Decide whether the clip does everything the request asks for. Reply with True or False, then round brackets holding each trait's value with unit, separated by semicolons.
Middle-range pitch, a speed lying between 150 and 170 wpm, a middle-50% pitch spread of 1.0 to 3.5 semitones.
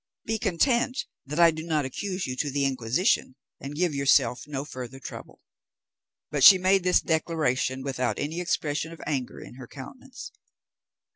False (150 Hz; 160 wpm; 5.2 semitones)